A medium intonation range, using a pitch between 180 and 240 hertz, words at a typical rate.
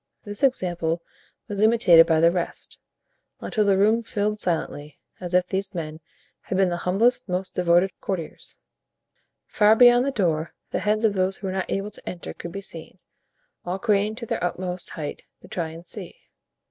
Yes: average, 3.4 semitones; high, 190 Hz; average, 180 wpm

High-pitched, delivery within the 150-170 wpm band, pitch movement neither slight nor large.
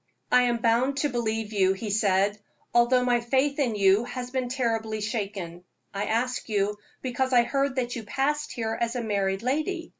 No: high, 235 Hz; average, 185 wpm; average, 3.5 semitones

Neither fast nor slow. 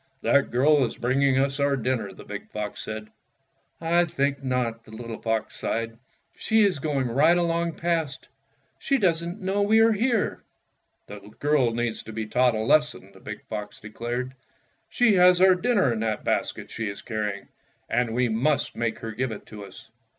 Yes: average, 185 wpm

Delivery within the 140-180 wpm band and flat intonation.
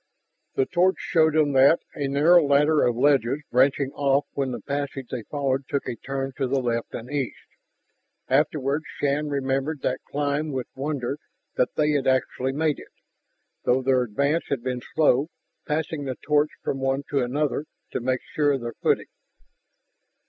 Yes: average, 170 wpm; narrow, 2.1 semitones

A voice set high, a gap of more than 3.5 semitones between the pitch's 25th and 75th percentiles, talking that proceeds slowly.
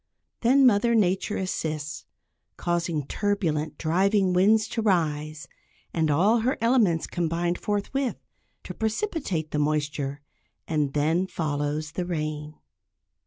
No: medium, 175 Hz; average, 5.2 semitones; slow, 115 wpm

